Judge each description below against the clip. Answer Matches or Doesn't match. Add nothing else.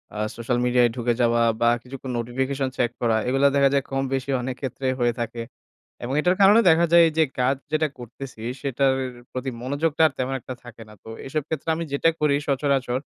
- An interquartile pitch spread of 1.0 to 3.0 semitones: Matches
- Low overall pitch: Matches